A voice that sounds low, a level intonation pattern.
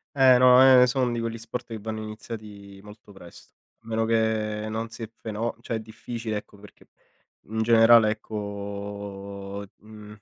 Yes: low, 110 Hz; narrow, 1.9 semitones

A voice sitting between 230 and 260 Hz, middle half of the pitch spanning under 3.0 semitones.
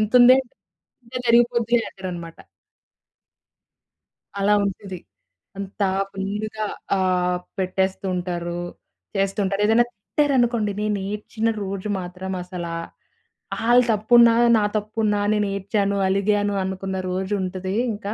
No: high, 200 Hz; narrow, 2.4 semitones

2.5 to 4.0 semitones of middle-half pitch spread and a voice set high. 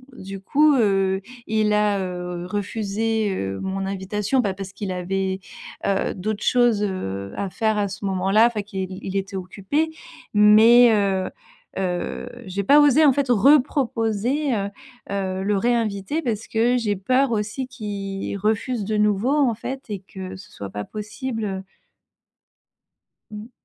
Yes: average, 3.3 semitones; high, 205 Hz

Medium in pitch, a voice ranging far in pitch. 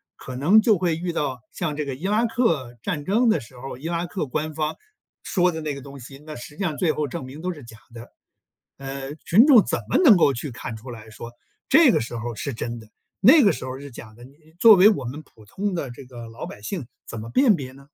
Yes: medium, 145 Hz; wide, 6.5 semitones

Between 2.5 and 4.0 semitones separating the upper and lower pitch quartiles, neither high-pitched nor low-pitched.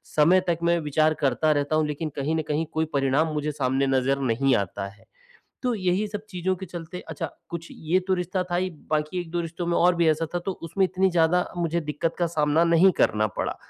Yes: average, 3.0 semitones; medium, 165 Hz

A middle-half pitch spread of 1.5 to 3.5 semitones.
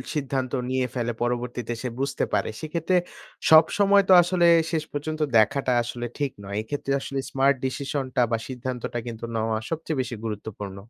No: average, 4.1 semitones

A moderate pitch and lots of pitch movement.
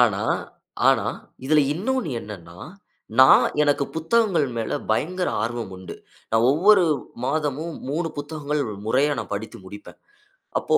Yes: medium, 145 Hz; wide, 6.3 semitones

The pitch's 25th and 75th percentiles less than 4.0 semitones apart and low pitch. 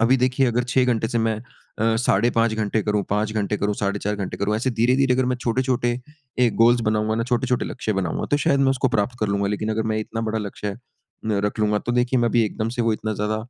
Yes: average, 2.7 semitones; low, 115 Hz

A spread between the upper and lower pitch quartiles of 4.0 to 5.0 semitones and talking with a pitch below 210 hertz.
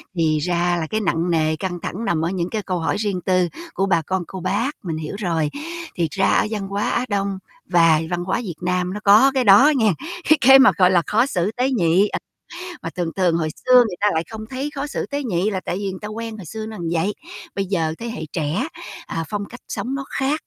Yes: average, 4.3 semitones; high, 190 Hz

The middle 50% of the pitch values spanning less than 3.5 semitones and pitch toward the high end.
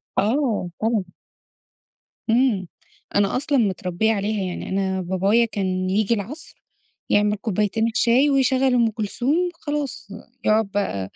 No: average, 3.9 semitones; high, 215 Hz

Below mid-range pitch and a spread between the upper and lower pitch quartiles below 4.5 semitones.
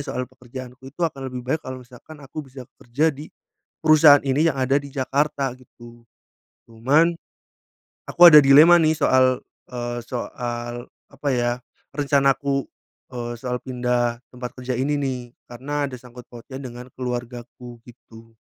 Yes: low, 130 Hz; narrow, 2.6 semitones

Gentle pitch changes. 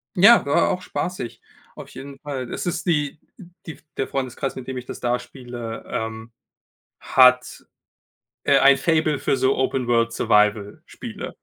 No: average, 3.7 semitones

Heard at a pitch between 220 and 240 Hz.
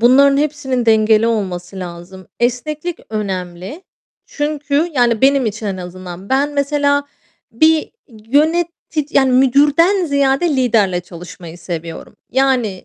No: very high, 250 Hz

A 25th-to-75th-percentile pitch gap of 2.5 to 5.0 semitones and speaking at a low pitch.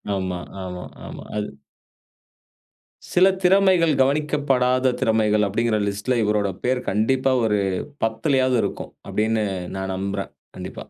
Yes: average, 4.3 semitones; low, 115 Hz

